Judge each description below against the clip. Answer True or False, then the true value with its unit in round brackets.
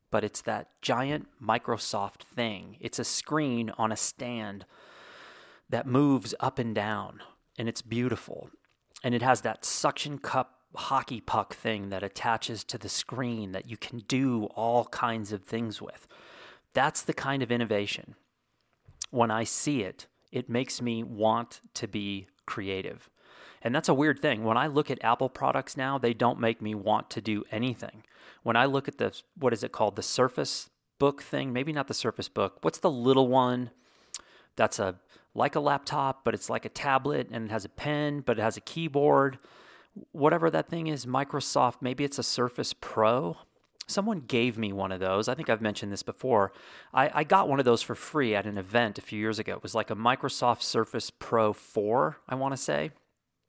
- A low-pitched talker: True (120 Hz)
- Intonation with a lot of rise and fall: False (3.5 semitones)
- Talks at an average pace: True (190 wpm)